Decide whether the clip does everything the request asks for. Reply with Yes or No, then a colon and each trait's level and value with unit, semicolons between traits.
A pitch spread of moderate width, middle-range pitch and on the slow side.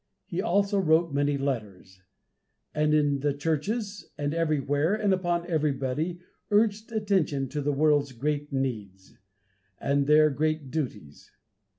Yes: average, 3.8 semitones; medium, 150 Hz; slow, 125 wpm